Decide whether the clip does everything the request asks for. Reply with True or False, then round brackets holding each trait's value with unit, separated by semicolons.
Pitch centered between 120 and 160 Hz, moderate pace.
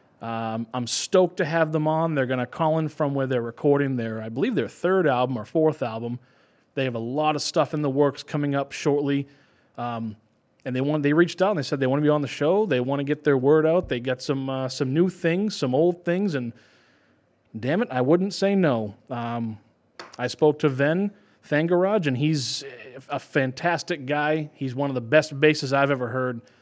False (140 Hz; 220 wpm)